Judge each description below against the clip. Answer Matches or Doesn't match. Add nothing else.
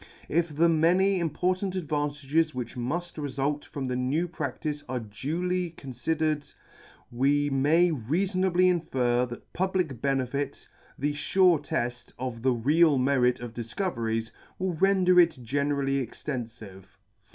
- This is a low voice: Doesn't match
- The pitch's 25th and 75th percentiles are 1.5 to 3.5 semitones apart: Doesn't match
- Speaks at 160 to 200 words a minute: Doesn't match